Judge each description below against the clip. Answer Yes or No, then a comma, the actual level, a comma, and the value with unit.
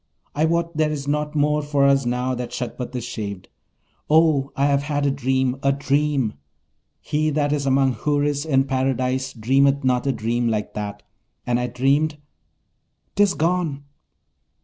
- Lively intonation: No, average, 2.7 semitones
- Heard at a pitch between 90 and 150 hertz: Yes, medium, 140 Hz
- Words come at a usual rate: Yes, average, 160 wpm